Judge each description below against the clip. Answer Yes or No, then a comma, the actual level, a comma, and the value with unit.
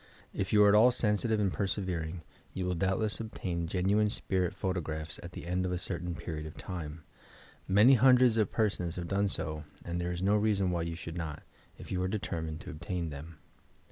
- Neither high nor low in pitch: No, very low, 90 Hz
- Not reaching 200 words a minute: No, fast, 205 wpm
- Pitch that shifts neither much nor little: Yes, average, 3.5 semitones